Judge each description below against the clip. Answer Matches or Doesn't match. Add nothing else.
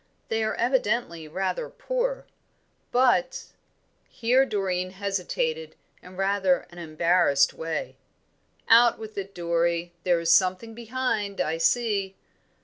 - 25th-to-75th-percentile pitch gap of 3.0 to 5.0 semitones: Doesn't match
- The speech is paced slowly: Matches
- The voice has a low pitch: Doesn't match